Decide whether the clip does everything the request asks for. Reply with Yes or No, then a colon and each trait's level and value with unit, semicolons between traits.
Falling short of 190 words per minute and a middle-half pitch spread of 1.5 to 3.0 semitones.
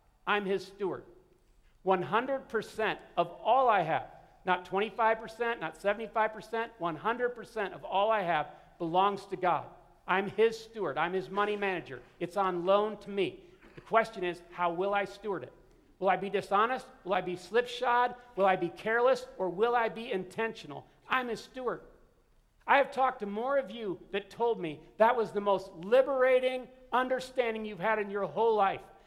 No: average, 170 wpm; average, 3.7 semitones